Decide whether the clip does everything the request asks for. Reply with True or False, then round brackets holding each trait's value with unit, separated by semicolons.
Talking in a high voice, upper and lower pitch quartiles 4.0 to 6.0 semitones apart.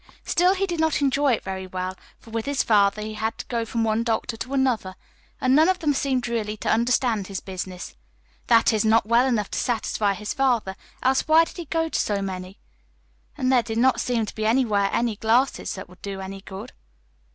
True (225 Hz; 4.5 semitones)